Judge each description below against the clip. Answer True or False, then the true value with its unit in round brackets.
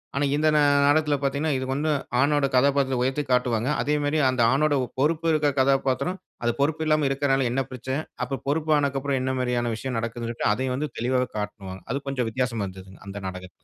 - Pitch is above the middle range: False (135 Hz)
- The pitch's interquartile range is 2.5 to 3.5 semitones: True (2.9 semitones)